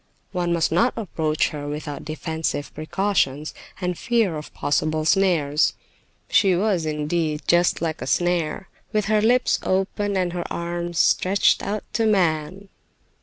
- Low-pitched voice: No, medium, 175 Hz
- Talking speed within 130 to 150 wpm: Yes, average, 140 wpm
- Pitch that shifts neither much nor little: Yes, average, 4.0 semitones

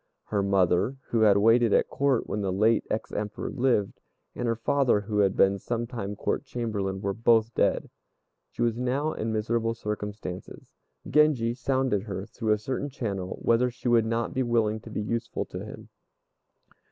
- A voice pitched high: No, low, 115 Hz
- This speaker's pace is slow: No, average, 175 wpm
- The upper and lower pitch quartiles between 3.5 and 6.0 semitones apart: No, average, 2.7 semitones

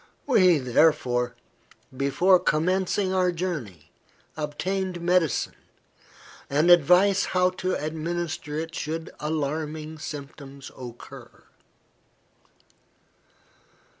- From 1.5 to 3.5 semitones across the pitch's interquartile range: No, average, 3.9 semitones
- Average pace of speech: No, slow, 75 wpm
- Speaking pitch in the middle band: Yes, medium, 160 Hz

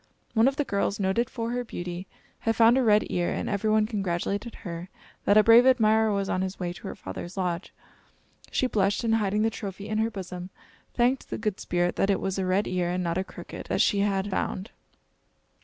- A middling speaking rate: No, fast, 220 wpm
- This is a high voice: Yes, high, 200 Hz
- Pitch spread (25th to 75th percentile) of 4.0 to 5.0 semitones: No, average, 3.3 semitones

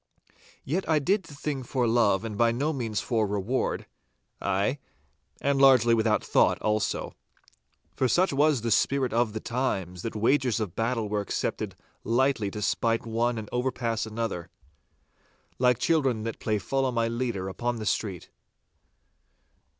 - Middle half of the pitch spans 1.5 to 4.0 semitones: Yes, average, 3.5 semitones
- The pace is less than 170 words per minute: Yes, average, 150 wpm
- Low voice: Yes, low, 115 Hz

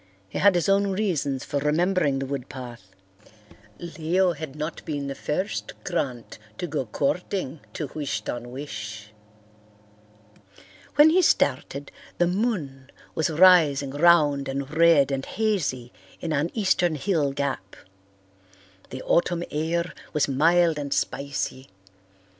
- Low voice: No, medium, 150 Hz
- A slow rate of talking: Yes, slow, 130 wpm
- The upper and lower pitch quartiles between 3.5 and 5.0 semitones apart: Yes, average, 4.2 semitones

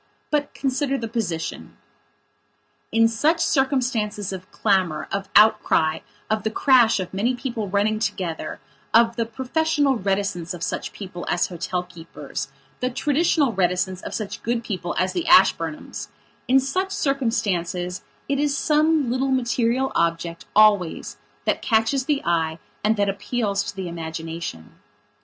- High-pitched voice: Yes, high, 215 Hz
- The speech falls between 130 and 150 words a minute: Yes, average, 140 wpm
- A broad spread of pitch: Yes, wide, 6.3 semitones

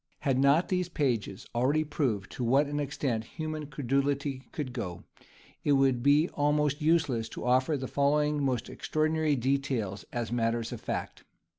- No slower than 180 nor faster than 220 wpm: No, average, 155 wpm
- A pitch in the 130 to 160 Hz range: Yes, medium, 140 Hz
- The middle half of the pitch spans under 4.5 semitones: Yes, average, 3.3 semitones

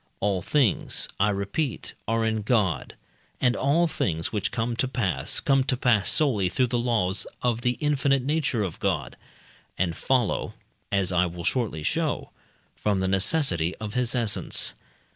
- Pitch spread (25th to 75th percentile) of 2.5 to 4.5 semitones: No, average, 5.1 semitones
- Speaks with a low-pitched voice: Yes, low, 110 Hz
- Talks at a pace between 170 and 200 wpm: No, average, 160 wpm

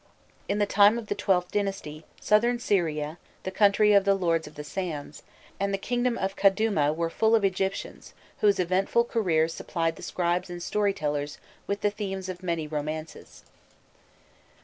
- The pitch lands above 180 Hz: Yes, high, 190 Hz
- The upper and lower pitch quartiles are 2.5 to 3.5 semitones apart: No, average, 3.9 semitones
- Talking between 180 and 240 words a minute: No, average, 165 wpm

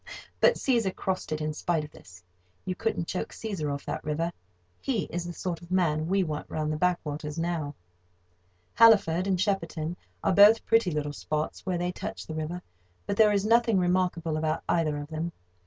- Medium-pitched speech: Yes, medium, 170 Hz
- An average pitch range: Yes, average, 3.6 semitones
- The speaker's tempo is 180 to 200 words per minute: Yes, average, 185 wpm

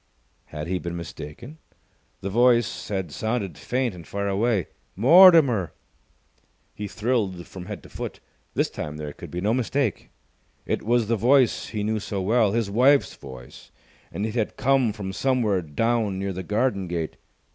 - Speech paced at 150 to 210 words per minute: Yes, average, 165 wpm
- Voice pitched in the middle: No, low, 105 Hz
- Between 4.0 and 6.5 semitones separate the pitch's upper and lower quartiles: Yes, average, 4.6 semitones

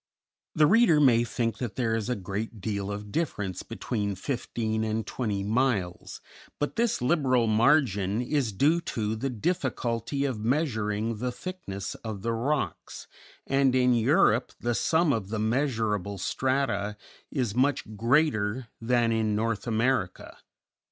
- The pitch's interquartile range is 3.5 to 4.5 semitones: Yes, average, 4.1 semitones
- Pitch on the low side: Yes, low, 115 Hz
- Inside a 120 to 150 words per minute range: Yes, average, 140 wpm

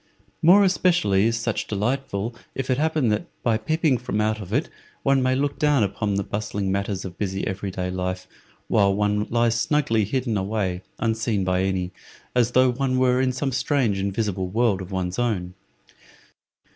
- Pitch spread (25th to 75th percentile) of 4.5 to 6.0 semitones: Yes, average, 4.8 semitones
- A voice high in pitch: No, low, 110 Hz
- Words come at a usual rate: Yes, average, 170 wpm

